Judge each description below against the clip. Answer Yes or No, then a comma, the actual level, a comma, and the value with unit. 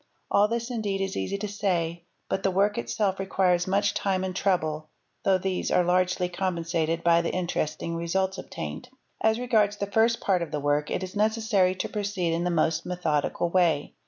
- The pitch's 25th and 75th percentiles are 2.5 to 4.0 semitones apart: Yes, average, 3.0 semitones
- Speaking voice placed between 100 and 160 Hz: No, medium, 185 Hz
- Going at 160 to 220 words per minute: Yes, average, 190 wpm